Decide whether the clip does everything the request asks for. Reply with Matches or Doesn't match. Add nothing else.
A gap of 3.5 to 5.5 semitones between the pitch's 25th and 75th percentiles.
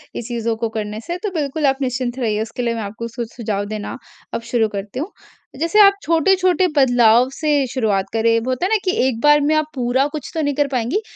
Matches